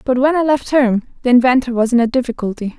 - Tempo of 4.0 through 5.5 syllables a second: No, 6.4 syllables/s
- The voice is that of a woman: Yes, female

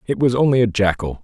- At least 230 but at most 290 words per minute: Yes, fast, 240 wpm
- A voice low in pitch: Yes, low, 115 Hz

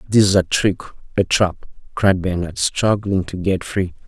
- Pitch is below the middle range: Yes, very low, 95 Hz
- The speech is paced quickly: No, average, 160 wpm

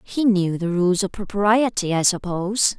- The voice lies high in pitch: Yes, high, 195 Hz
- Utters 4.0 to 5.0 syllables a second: Yes, 4.5 syllables/s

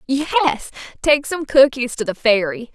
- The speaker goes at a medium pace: Yes, average, 155 wpm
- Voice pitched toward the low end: No, very high, 260 Hz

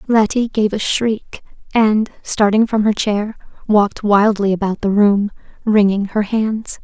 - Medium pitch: No, high, 210 Hz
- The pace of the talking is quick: No, average, 150 wpm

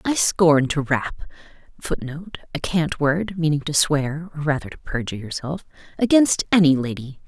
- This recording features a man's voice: No, female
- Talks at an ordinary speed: Yes, average, 155 wpm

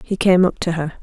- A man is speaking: No, female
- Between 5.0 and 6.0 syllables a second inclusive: Yes, 5.9 syllables/s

